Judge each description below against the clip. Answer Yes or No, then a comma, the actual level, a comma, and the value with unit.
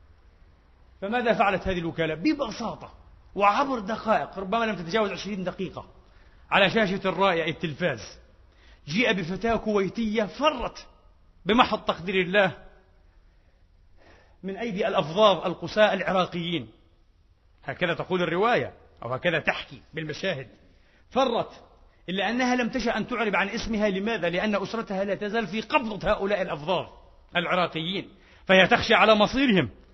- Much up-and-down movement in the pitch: Yes, wide, 7.1 semitones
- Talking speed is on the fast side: No, average, 115 wpm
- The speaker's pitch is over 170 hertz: Yes, medium, 185 Hz